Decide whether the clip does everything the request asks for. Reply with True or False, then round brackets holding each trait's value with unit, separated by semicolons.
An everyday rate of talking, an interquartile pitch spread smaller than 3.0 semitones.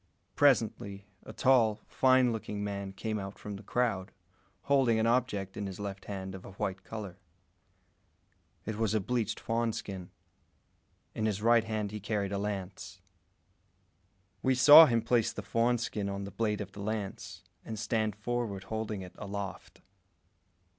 True (160 wpm; 2.6 semitones)